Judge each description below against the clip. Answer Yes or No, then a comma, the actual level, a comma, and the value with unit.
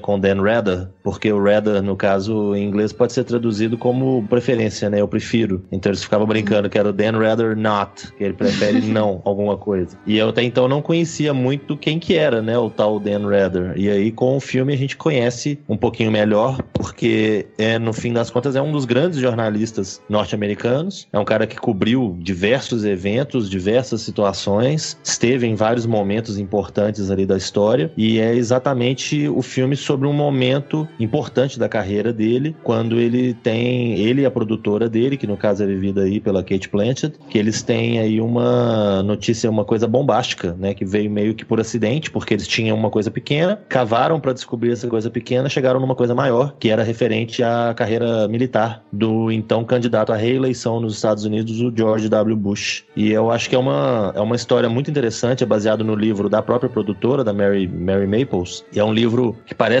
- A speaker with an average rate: No, fast, 195 wpm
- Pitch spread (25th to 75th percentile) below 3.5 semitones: Yes, average, 3.1 semitones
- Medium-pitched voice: No, low, 115 Hz